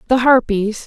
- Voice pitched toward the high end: Yes, high, 230 Hz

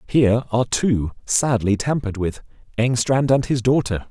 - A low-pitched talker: Yes, low, 120 Hz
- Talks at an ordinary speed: Yes, average, 145 wpm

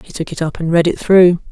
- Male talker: No, female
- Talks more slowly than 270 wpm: No, fast, 315 wpm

